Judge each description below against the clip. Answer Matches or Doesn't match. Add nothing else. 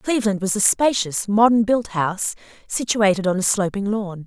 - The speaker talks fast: Doesn't match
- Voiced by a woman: Matches